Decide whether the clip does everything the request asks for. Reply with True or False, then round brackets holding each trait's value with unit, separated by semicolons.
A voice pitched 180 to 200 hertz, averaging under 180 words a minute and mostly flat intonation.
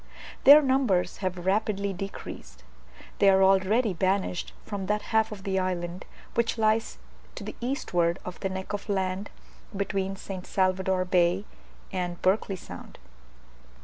True (190 Hz; 140 wpm; 2.2 semitones)